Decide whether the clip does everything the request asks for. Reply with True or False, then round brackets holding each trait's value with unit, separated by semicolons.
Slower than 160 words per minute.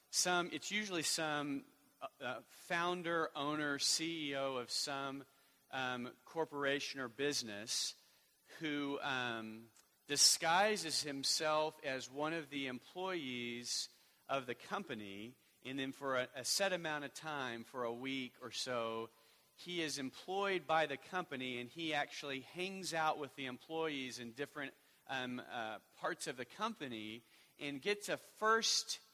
True (135 wpm)